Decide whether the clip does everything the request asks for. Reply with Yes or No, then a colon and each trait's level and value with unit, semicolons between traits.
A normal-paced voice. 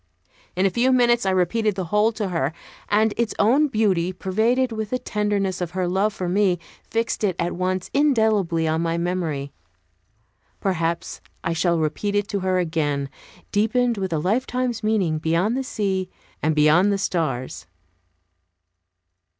Yes: average, 160 wpm